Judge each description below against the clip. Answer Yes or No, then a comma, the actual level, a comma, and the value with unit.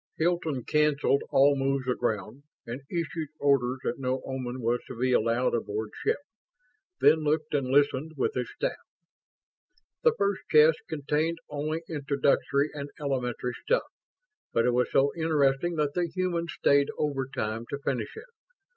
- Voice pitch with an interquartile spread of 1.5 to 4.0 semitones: Yes, average, 3.5 semitones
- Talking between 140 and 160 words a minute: Yes, average, 145 wpm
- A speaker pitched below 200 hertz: Yes, medium, 140 Hz